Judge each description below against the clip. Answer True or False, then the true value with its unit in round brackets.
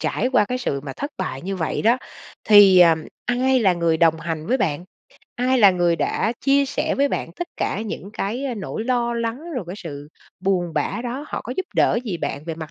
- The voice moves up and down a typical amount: False (6.6 semitones)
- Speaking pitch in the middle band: False (205 Hz)